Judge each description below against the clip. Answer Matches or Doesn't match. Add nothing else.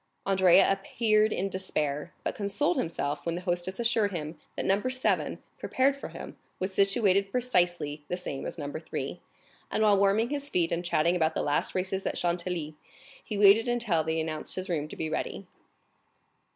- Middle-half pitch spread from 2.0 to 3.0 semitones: Doesn't match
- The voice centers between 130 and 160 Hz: Doesn't match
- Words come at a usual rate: Matches